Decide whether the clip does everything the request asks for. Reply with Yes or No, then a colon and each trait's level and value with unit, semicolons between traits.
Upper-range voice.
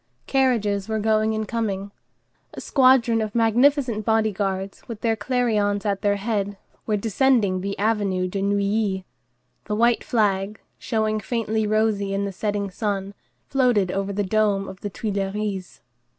Yes: high, 210 Hz